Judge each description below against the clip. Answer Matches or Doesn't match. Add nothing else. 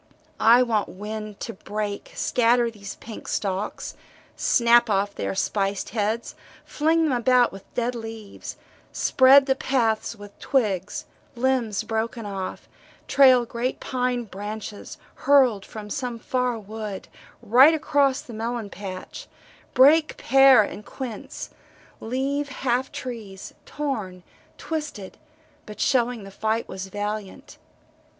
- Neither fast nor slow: Doesn't match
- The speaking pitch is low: Doesn't match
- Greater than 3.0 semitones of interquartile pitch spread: Matches